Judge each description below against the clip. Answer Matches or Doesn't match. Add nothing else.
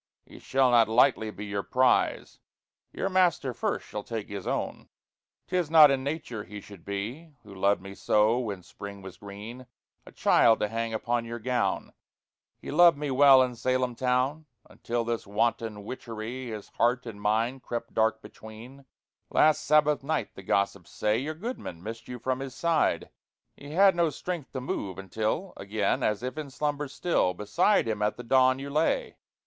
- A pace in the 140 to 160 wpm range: Doesn't match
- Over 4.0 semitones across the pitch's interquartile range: Matches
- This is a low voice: Matches